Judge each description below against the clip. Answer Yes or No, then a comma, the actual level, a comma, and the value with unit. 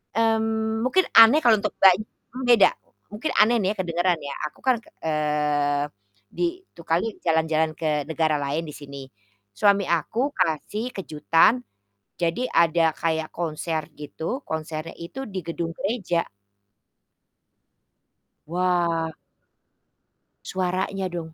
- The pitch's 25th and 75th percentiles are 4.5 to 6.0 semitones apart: Yes, average, 5.2 semitones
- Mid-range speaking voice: Yes, medium, 170 Hz